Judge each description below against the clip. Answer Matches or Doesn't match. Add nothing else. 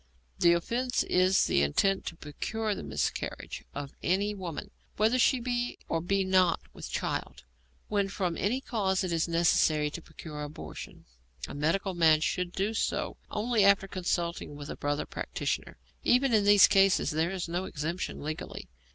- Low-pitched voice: Doesn't match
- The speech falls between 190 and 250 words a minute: Doesn't match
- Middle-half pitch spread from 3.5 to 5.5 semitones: Matches